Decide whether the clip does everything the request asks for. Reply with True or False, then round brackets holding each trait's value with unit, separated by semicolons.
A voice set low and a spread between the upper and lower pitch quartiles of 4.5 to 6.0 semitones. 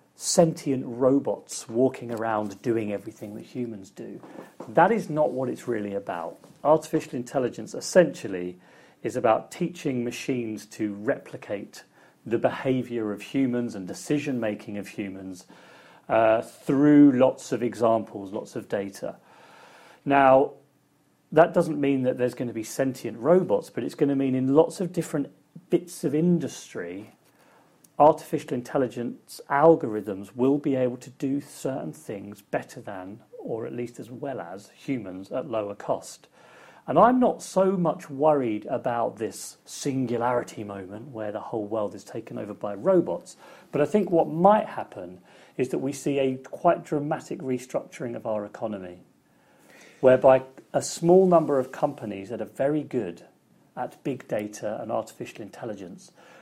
True (130 Hz; 5.2 semitones)